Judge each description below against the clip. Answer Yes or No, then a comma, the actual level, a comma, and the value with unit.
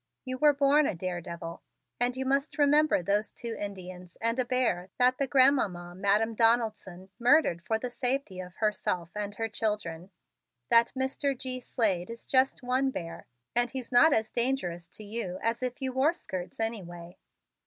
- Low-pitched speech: No, high, 230 Hz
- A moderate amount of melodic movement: No, wide, 5.8 semitones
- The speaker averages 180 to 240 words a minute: No, average, 165 wpm